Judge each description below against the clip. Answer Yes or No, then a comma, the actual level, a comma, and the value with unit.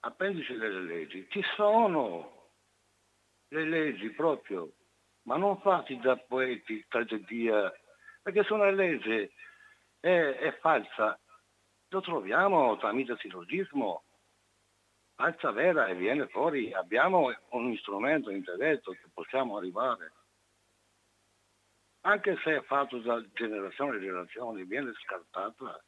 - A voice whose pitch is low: Yes, low, 130 Hz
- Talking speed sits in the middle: No, slow, 110 wpm